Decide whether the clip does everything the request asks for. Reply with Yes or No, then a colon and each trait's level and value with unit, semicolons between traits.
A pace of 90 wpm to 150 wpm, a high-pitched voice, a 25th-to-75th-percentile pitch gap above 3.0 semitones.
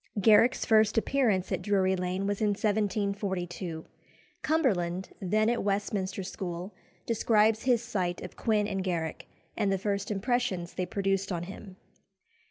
No: average, 140 wpm; high, 200 Hz; average, 2.7 semitones